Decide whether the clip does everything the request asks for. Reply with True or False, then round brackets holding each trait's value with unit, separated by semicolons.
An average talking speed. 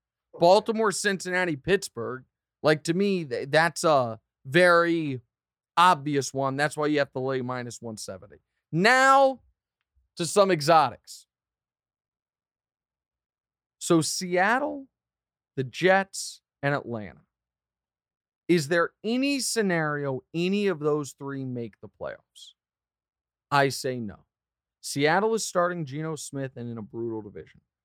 False (115 wpm)